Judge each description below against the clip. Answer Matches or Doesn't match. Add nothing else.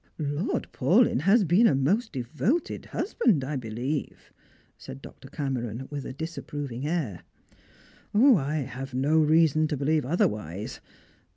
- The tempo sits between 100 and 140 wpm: Matches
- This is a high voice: Doesn't match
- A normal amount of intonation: Matches